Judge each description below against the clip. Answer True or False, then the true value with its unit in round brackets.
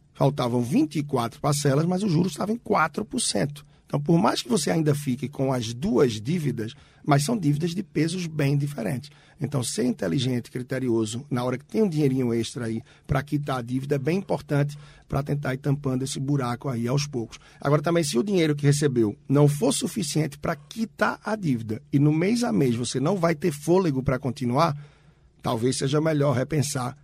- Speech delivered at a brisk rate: True (190 wpm)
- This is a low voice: False (145 Hz)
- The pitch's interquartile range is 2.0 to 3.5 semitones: False (3.9 semitones)